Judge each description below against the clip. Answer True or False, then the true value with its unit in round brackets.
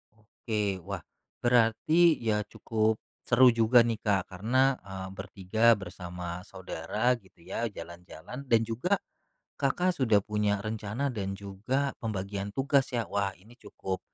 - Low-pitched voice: True (110 Hz)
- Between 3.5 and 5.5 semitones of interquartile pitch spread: True (3.8 semitones)